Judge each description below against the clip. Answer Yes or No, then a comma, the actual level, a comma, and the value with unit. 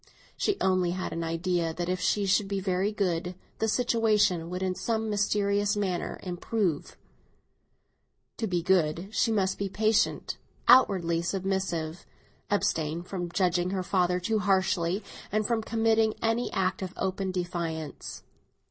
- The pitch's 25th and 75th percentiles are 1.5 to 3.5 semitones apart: Yes, average, 2.8 semitones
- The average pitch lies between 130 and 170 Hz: No, high, 190 Hz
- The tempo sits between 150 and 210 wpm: No, average, 140 wpm